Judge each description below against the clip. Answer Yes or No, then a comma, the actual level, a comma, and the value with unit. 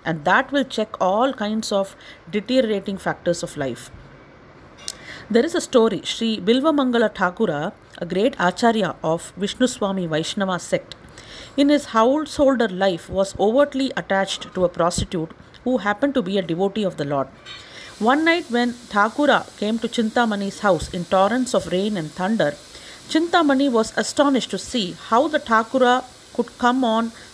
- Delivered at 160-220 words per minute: No, average, 150 wpm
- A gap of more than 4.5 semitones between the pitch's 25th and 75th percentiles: Yes, average, 5.1 semitones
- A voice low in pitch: No, high, 220 Hz